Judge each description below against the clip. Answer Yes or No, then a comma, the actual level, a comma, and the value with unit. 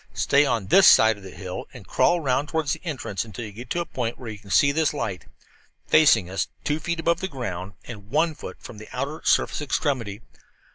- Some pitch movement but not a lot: No, wide, 6.8 semitones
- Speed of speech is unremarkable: No, fast, 230 wpm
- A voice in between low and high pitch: No, low, 125 Hz